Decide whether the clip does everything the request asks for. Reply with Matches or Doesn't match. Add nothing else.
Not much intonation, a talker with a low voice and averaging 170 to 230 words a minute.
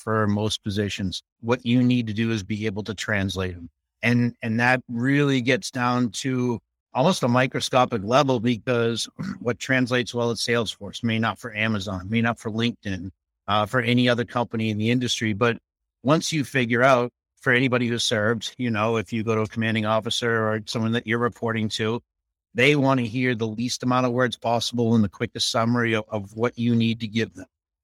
Matches